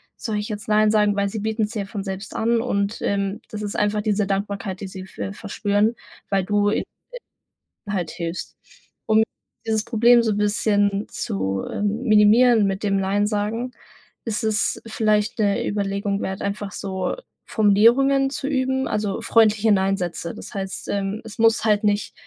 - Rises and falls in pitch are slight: Yes, narrow, 1.8 semitones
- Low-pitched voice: No, high, 210 Hz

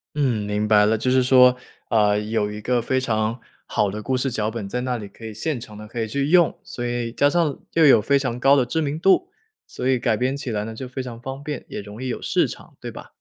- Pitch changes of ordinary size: Yes, average, 3.7 semitones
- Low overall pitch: Yes, low, 120 Hz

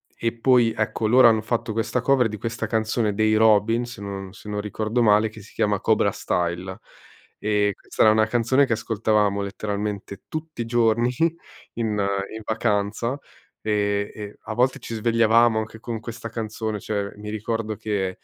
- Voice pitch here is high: No, low, 110 Hz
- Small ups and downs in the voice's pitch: Yes, narrow, 1.9 semitones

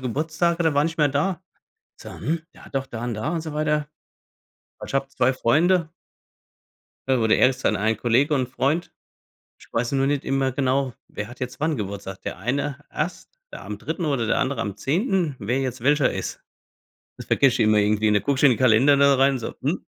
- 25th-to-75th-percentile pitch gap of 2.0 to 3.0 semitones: No, average, 3.9 semitones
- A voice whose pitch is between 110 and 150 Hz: Yes, low, 135 Hz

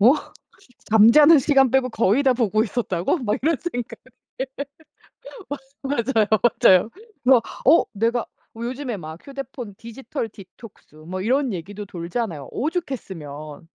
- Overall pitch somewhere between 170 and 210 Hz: No, high, 230 Hz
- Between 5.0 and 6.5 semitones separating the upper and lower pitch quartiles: Yes, wide, 5.6 semitones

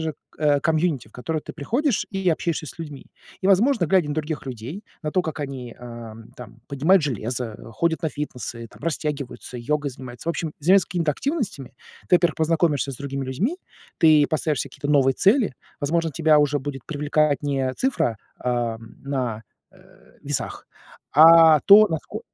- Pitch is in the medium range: Yes, medium, 150 Hz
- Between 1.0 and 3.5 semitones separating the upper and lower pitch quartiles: No, average, 4.0 semitones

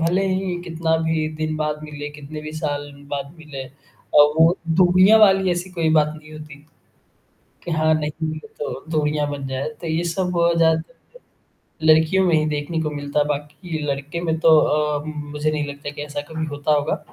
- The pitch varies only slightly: Yes, narrow, 1.8 semitones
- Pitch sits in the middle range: Yes, medium, 155 Hz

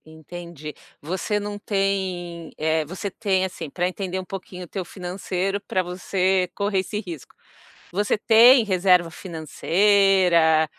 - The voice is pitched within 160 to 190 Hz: Yes, medium, 185 Hz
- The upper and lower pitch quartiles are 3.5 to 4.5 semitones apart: No, narrow, 2.4 semitones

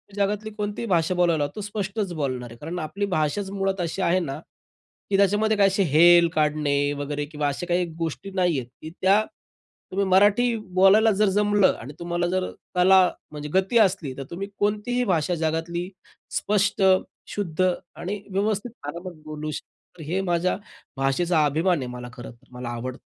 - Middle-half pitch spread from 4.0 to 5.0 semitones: Yes, average, 4.6 semitones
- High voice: No, medium, 180 Hz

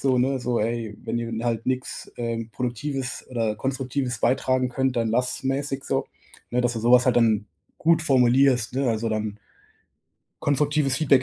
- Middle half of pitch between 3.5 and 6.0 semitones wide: No, narrow, 2.5 semitones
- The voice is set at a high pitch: No, low, 125 Hz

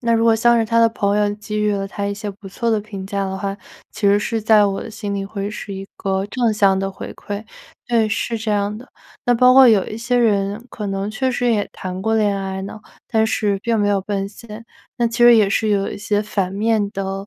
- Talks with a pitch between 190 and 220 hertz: Yes, high, 210 Hz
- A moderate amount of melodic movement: No, narrow, 2.2 semitones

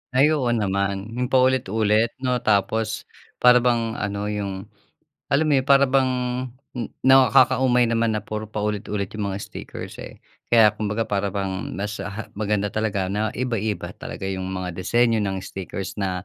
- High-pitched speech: No, low, 105 Hz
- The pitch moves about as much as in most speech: Yes, average, 3.3 semitones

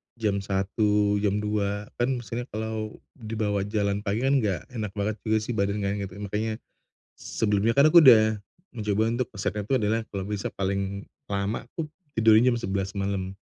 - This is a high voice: No, low, 105 Hz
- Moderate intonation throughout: No, narrow, 1.9 semitones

